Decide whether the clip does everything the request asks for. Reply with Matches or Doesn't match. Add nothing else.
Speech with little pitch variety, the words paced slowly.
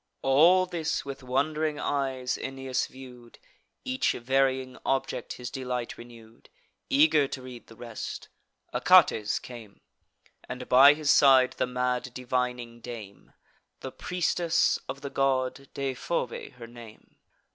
Matches